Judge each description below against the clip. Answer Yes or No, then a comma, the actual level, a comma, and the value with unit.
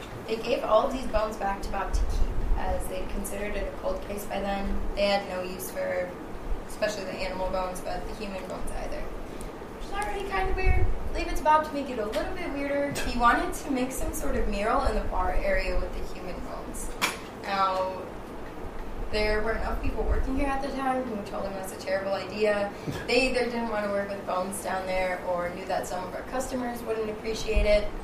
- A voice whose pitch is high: Yes, high, 215 Hz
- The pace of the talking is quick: Yes, fast, 225 wpm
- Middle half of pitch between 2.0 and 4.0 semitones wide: No, average, 4.9 semitones